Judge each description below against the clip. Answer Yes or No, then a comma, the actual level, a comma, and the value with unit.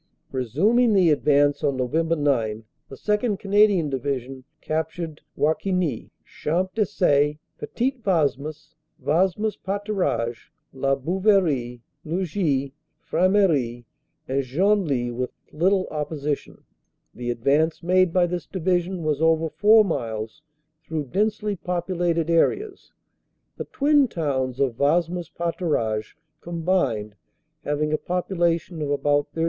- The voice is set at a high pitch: No, medium, 160 Hz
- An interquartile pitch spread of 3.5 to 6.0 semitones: Yes, average, 4.9 semitones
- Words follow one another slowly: Yes, slow, 110 wpm